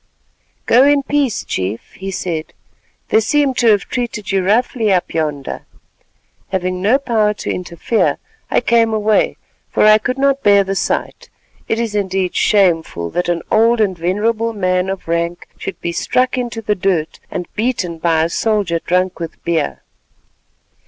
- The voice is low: No, high, 200 Hz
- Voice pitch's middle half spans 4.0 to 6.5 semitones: Yes, average, 4.6 semitones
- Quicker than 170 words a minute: No, average, 160 wpm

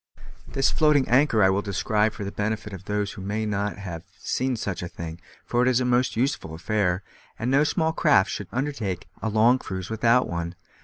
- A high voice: No, low, 105 Hz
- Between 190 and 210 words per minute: Yes, fast, 205 wpm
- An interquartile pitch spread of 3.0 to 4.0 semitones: No, average, 4.7 semitones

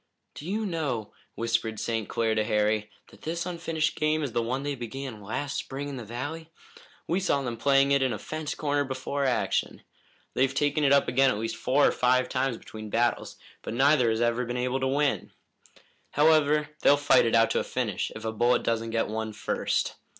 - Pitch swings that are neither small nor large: Yes, average, 4.0 semitones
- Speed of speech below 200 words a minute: No, fast, 205 wpm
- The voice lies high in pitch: No, low, 130 Hz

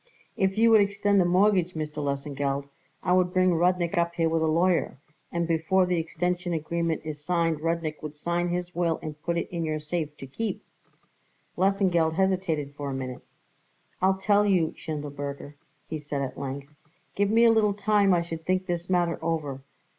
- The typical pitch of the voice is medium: Yes, medium, 170 Hz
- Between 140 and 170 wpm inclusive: No, average, 185 wpm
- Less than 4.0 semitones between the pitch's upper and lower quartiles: Yes, average, 3.3 semitones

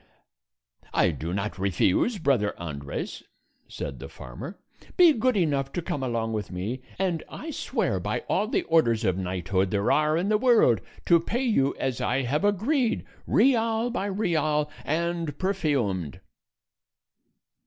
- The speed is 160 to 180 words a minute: No, average, 145 wpm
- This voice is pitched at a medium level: Yes, medium, 150 Hz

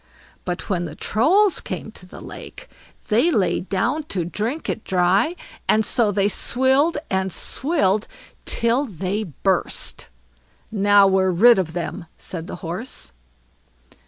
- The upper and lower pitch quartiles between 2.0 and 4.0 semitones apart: No, average, 4.6 semitones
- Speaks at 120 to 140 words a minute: Yes, slow, 135 wpm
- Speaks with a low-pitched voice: No, high, 200 Hz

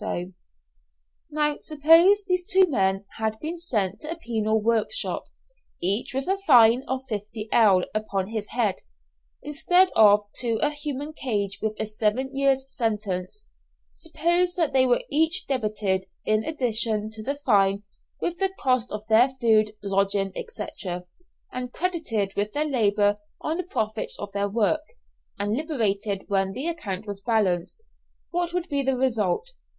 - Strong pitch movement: Yes, wide, 6.4 semitones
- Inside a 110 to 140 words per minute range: No, average, 150 wpm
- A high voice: Yes, high, 230 Hz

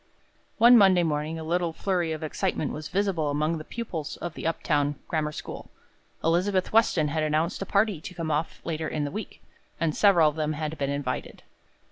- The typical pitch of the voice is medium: Yes, medium, 160 Hz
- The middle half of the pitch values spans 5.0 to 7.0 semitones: No, average, 3.0 semitones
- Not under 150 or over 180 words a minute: No, average, 195 wpm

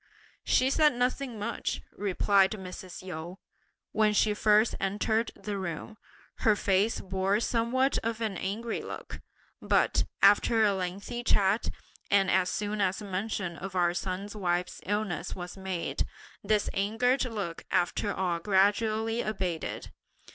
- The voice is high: Yes, high, 205 Hz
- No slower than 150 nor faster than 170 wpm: No, slow, 135 wpm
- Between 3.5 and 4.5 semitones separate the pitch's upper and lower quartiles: No, average, 2.8 semitones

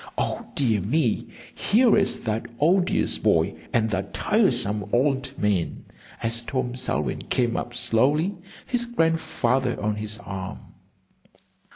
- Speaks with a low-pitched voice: Yes, low, 120 Hz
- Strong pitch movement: Yes, wide, 6.6 semitones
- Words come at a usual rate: No, slow, 125 wpm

